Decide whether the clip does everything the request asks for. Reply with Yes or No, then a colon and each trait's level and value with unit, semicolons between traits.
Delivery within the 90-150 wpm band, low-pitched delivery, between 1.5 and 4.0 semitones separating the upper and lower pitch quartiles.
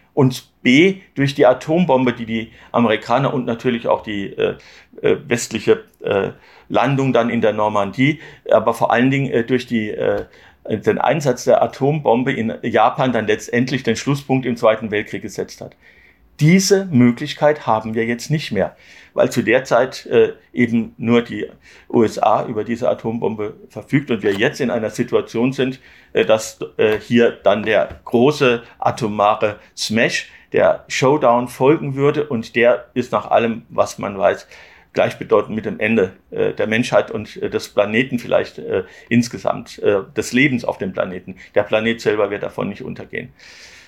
No: average, 160 wpm; low, 120 Hz; average, 3.6 semitones